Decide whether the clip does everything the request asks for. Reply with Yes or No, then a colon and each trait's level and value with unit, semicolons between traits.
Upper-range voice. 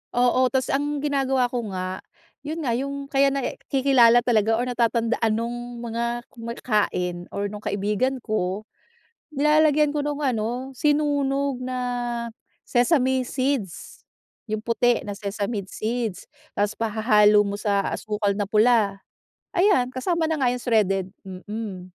Yes: high, 240 Hz